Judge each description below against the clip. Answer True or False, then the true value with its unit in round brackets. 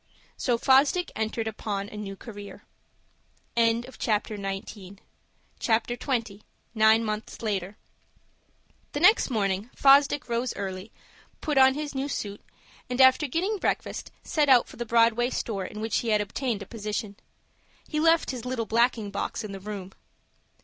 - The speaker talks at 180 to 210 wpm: False (145 wpm)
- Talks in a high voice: True (225 Hz)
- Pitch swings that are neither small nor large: True (4.2 semitones)